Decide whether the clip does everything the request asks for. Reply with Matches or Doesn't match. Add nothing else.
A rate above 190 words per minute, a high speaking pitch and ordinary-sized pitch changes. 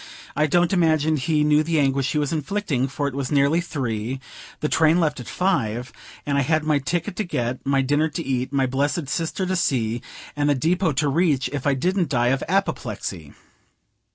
Doesn't match